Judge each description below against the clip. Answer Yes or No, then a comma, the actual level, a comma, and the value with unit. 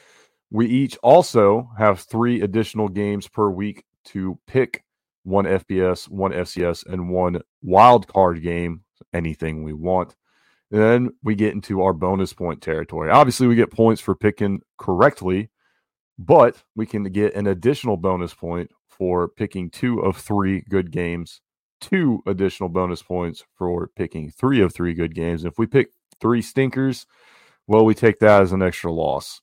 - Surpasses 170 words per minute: No, average, 160 wpm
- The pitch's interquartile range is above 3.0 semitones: Yes, average, 3.5 semitones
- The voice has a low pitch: Yes, very low, 95 Hz